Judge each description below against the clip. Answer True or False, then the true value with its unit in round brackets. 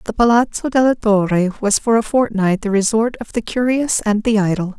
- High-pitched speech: True (220 Hz)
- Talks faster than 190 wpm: True (200 wpm)